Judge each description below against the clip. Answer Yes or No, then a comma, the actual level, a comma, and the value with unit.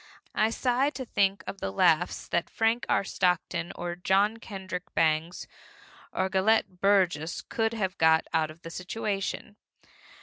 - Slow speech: No, average, 145 wpm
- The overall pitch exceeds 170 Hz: Yes, high, 190 Hz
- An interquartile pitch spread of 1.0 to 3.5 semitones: No, average, 4.0 semitones